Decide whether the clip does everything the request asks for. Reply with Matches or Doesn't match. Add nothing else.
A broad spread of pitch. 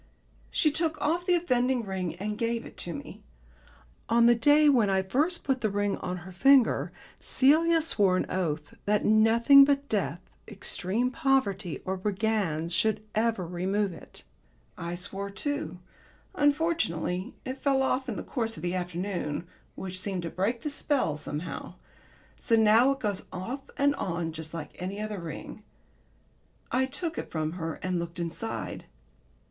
Matches